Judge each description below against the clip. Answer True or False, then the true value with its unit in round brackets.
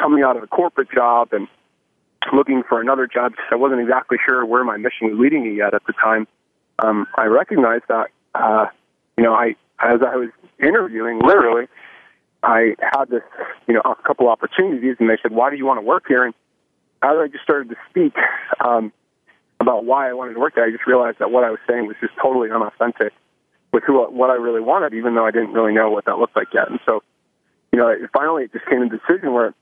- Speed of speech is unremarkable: False (225 wpm)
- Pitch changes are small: True (2.3 semitones)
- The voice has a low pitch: True (120 Hz)